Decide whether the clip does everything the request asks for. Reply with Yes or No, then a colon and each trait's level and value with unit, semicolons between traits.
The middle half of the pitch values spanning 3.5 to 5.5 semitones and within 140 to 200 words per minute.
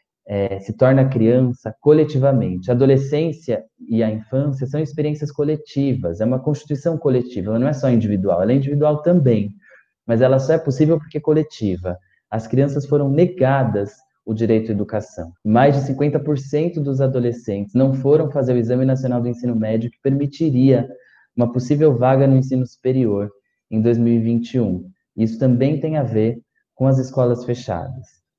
Yes: average, 4.1 semitones; average, 160 wpm